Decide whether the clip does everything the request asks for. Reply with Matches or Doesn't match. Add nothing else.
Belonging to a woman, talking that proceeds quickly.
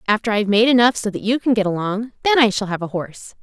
Matches